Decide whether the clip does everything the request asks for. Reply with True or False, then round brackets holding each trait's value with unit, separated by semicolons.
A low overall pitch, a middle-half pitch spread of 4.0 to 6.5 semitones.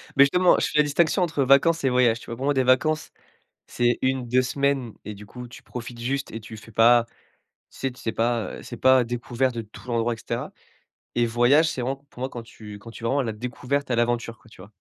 False (125 Hz; 2.7 semitones)